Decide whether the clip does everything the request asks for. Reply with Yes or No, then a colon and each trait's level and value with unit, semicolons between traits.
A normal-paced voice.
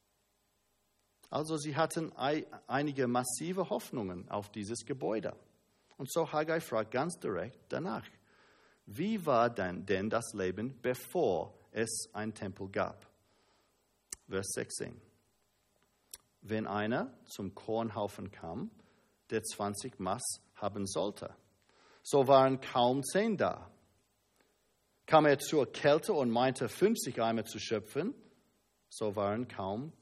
No: slow, 115 wpm